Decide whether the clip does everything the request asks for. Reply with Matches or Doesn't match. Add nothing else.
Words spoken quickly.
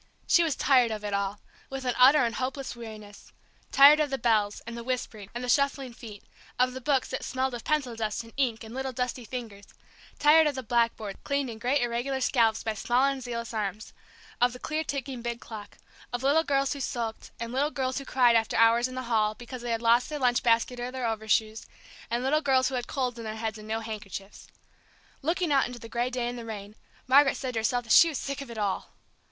Matches